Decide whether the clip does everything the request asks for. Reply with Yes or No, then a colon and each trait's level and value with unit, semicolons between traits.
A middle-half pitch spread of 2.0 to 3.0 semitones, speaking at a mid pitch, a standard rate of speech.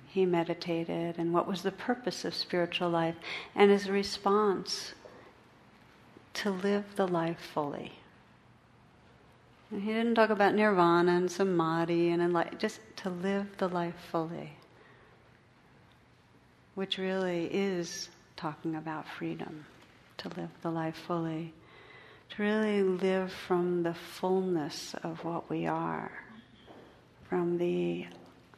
No: average, 2.7 semitones; medium, 175 Hz; slow, 120 wpm